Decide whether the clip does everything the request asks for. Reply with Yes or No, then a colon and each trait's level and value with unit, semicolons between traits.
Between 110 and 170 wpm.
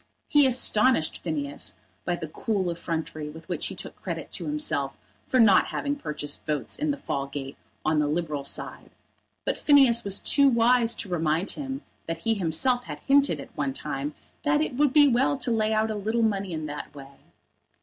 No: average, 190 wpm